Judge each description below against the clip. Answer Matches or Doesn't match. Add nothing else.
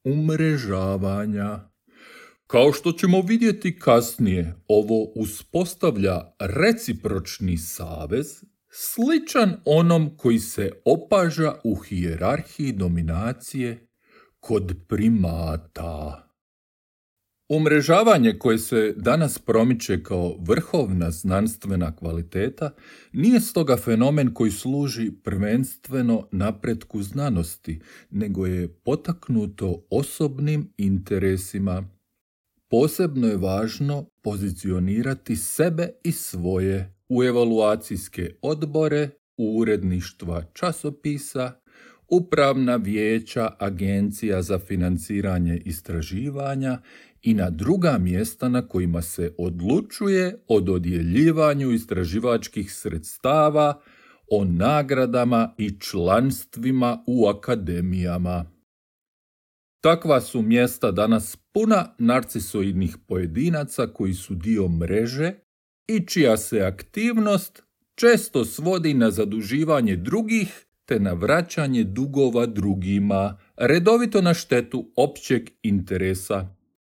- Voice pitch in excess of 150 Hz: Doesn't match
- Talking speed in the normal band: Doesn't match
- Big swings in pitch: Matches